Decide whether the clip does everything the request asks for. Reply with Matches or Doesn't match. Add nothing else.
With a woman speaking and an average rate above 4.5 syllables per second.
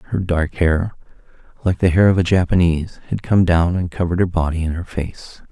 Doesn't match